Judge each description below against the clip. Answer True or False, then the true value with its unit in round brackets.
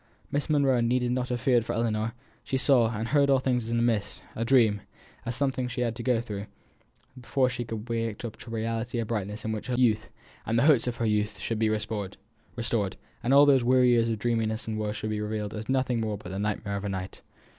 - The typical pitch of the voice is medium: False (115 Hz)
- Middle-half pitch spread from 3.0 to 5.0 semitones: False (2.5 semitones)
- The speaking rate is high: True (240 wpm)